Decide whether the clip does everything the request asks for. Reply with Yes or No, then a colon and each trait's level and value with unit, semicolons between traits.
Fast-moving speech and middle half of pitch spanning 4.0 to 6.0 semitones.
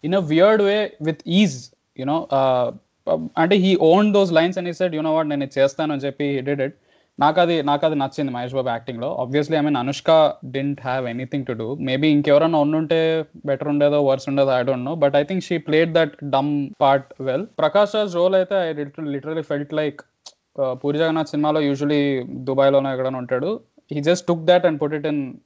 No: fast, 200 wpm; average, 2.9 semitones